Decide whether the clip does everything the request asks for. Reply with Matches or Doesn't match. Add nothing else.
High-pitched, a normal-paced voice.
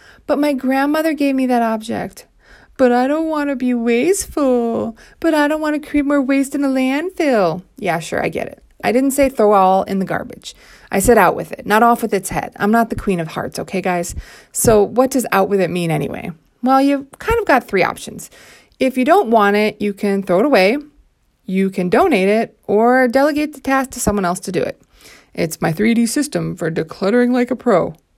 Doesn't match